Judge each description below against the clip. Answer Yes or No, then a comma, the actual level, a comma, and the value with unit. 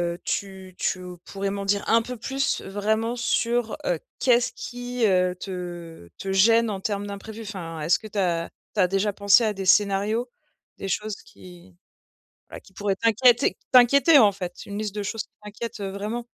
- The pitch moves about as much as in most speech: Yes, average, 3.0 semitones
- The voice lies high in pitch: Yes, high, 205 Hz